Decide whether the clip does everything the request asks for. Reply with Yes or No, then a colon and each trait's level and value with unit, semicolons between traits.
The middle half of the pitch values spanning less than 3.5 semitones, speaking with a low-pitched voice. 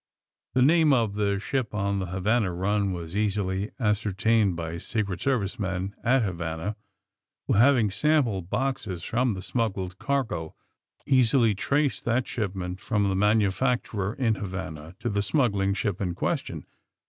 No: average, 4.0 semitones; low, 105 Hz